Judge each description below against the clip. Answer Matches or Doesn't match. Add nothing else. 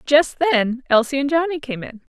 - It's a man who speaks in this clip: Doesn't match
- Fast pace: Doesn't match